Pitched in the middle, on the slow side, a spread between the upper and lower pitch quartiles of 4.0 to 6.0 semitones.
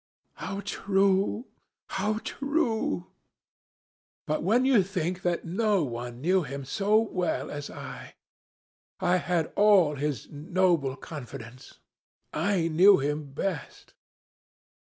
Yes: medium, 180 Hz; slow, 110 wpm; average, 5.3 semitones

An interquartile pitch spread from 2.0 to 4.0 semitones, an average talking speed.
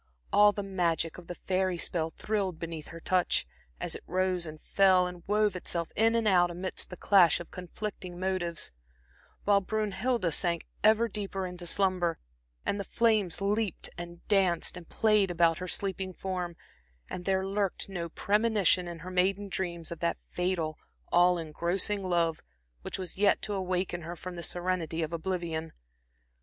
Yes: narrow, 2.4 semitones; average, 165 wpm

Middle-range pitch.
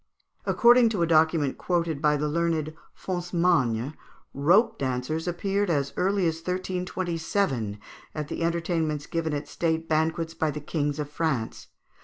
Yes: medium, 160 Hz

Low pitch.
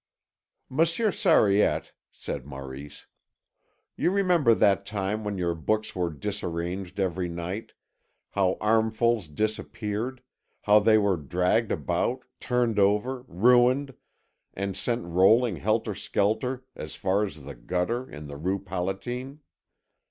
Yes: low, 105 Hz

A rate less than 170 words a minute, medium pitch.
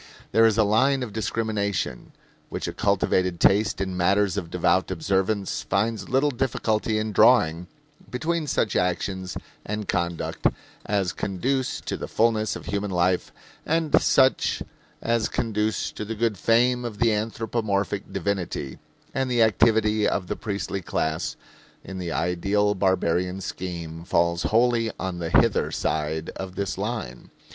No: average, 145 wpm; low, 100 Hz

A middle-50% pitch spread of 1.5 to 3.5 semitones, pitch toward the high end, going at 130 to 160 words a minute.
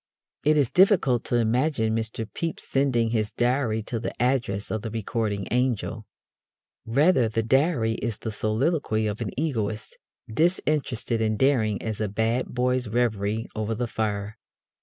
No: average, 2.9 semitones; low, 115 Hz; average, 150 wpm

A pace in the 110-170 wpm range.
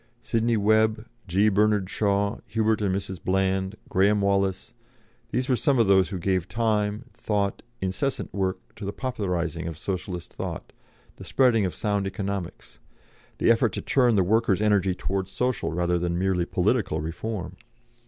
Yes: average, 155 wpm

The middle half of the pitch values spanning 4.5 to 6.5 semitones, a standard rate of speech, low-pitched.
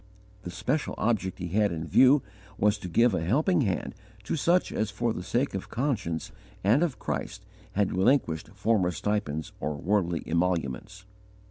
Yes: average, 5.2 semitones; average, 160 wpm; low, 100 Hz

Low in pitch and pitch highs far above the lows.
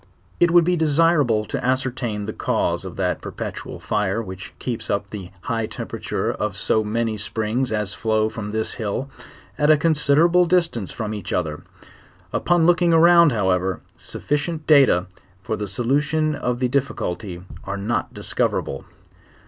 Yes: low, 120 Hz; wide, 6.6 semitones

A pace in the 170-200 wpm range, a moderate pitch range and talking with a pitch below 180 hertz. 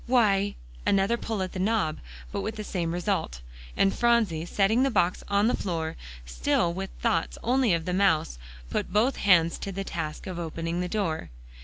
No: average, 185 wpm; average, 4.1 semitones; high, 195 Hz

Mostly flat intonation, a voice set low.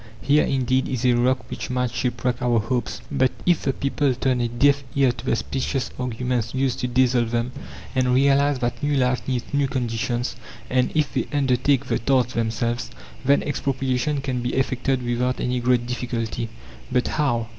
Yes: narrow, 1.9 semitones; low, 125 Hz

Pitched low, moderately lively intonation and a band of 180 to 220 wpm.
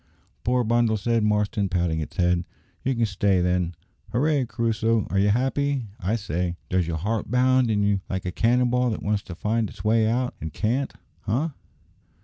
Yes: low, 110 Hz; average, 4.4 semitones; average, 185 wpm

